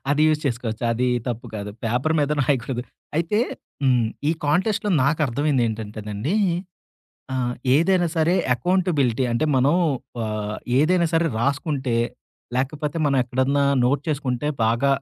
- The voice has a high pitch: No, low, 135 Hz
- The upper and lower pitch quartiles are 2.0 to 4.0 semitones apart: No, average, 4.4 semitones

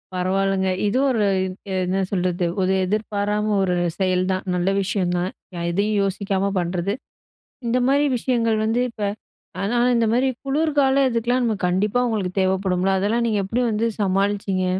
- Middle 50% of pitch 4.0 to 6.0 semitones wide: No, average, 3.5 semitones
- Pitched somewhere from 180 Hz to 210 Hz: Yes, high, 200 Hz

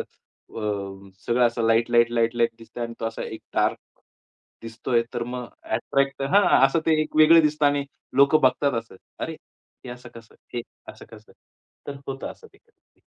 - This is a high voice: No, low, 125 Hz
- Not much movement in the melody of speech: No, average, 3.5 semitones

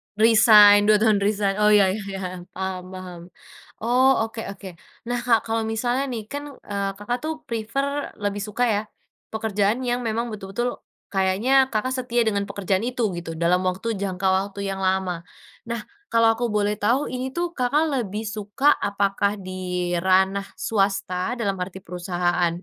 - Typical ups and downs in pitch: Yes, average, 3.5 semitones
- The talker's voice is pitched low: No, high, 205 Hz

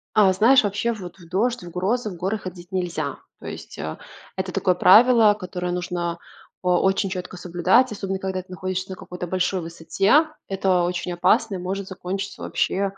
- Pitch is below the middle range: No, medium, 185 Hz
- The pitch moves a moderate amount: No, narrow, 1.9 semitones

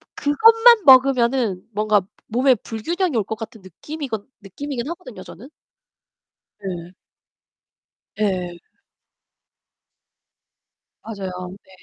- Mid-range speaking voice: No, high, 225 Hz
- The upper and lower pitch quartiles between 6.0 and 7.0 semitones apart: Yes, wide, 6.3 semitones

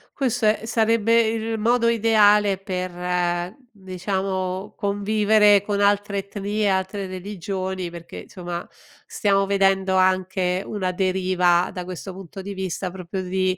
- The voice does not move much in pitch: Yes, narrow, 2.0 semitones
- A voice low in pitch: No, high, 195 Hz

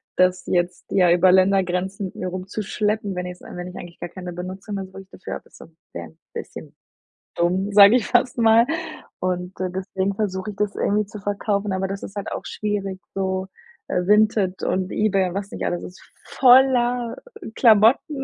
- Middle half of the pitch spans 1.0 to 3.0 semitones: Yes, narrow, 2.4 semitones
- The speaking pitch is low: No, high, 195 Hz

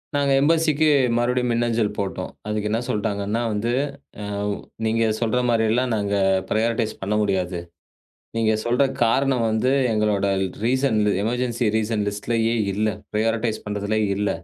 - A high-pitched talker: No, low, 110 Hz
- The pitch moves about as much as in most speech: No, narrow, 2.2 semitones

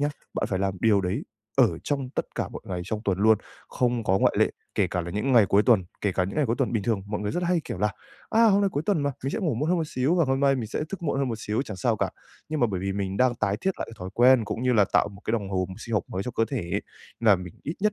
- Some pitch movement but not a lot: No, wide, 5.8 semitones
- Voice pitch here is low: Yes, low, 115 Hz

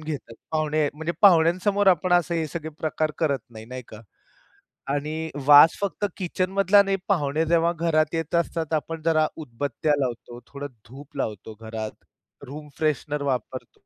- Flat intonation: No, average, 3.0 semitones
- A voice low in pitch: No, medium, 155 Hz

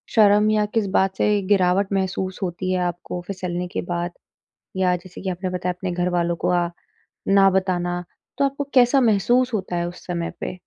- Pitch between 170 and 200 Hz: Yes, medium, 185 Hz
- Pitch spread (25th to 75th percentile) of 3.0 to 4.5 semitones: No, narrow, 2.5 semitones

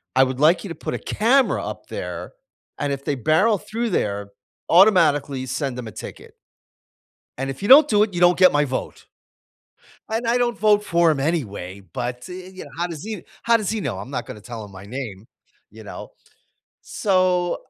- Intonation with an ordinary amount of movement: No, wide, 8.5 semitones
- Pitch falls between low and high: Yes, medium, 160 Hz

